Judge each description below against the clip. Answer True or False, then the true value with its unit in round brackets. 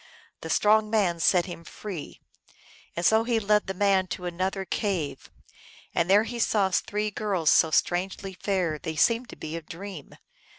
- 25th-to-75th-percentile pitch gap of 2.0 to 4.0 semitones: True (3.5 semitones)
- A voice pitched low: False (190 Hz)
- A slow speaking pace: False (170 wpm)